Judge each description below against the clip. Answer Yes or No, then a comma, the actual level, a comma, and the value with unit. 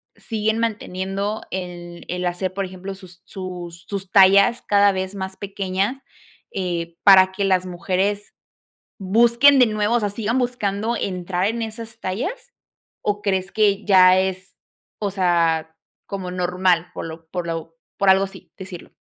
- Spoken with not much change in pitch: Yes, narrow, 2.2 semitones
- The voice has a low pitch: No, high, 190 Hz